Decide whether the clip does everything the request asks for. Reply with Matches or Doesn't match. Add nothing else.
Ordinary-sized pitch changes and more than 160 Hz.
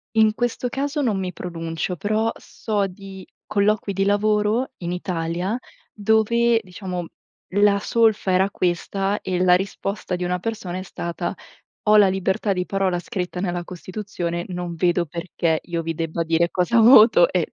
Matches